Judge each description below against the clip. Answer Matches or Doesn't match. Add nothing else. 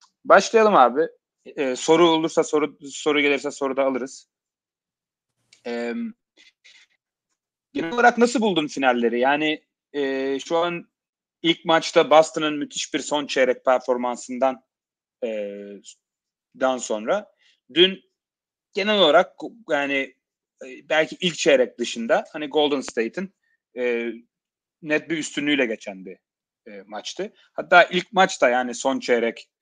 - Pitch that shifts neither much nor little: Matches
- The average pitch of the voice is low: Doesn't match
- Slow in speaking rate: Doesn't match